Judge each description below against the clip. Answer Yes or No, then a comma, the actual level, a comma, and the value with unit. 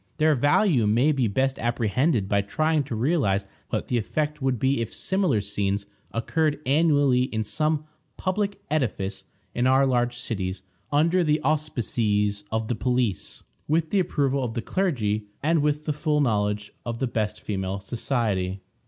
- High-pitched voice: No, low, 125 Hz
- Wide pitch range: Yes, wide, 6.2 semitones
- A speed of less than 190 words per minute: Yes, average, 160 wpm